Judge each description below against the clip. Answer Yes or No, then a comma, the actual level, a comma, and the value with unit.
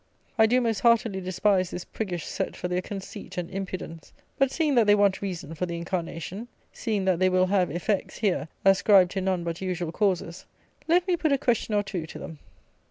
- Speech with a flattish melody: No, average, 3.3 semitones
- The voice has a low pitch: No, high, 190 Hz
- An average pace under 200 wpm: No, fast, 205 wpm